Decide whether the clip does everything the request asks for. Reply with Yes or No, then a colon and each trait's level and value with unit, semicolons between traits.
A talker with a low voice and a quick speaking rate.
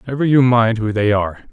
Yes: low, 115 Hz; fast, 235 wpm